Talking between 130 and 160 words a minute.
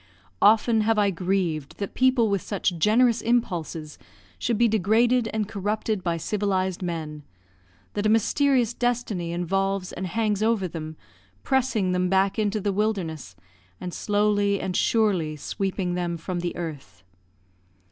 Yes: average, 140 wpm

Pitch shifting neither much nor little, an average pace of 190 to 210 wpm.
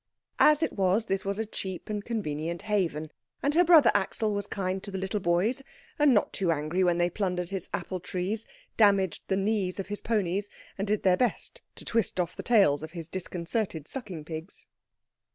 Yes: average, 3.3 semitones; average, 195 wpm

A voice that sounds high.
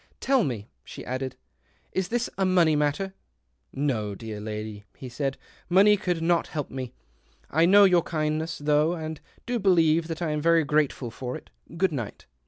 No: medium, 155 Hz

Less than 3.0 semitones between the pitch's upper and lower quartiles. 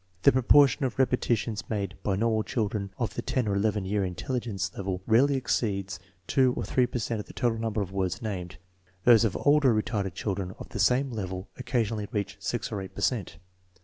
No: average, 3.7 semitones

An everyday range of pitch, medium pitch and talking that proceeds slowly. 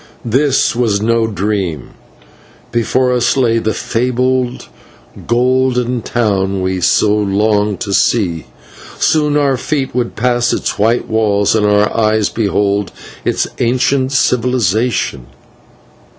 No: average, 3.4 semitones; low, 115 Hz; slow, 120 wpm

